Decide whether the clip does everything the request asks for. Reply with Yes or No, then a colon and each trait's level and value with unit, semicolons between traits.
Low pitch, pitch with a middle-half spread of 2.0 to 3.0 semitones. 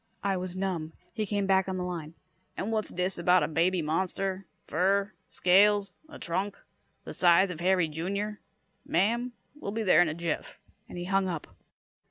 No: medium, 185 Hz; narrow, 2.5 semitones